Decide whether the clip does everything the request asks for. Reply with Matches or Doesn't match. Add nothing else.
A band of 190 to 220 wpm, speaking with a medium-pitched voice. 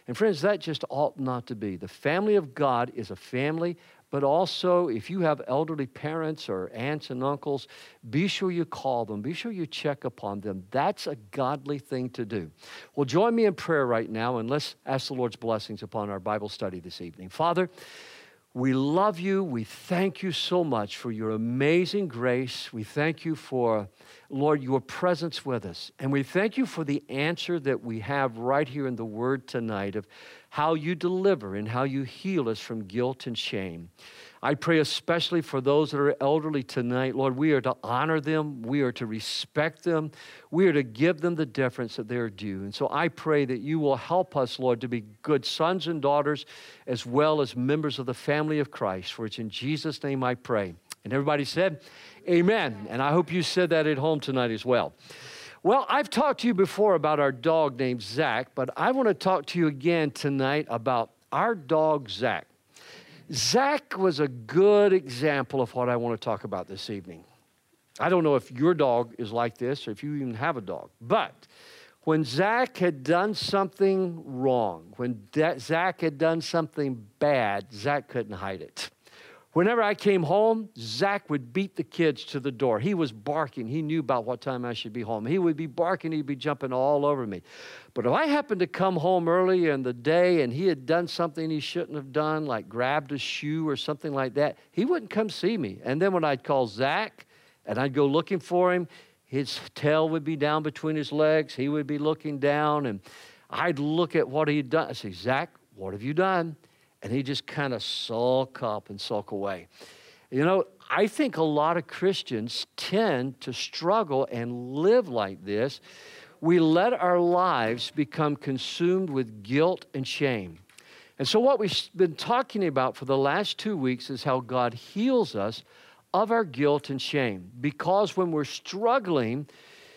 Matches